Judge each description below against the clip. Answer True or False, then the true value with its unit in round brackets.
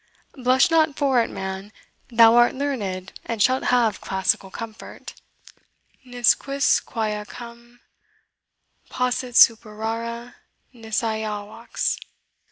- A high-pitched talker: True (230 Hz)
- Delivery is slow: True (95 wpm)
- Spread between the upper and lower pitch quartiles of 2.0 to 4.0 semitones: True (2.7 semitones)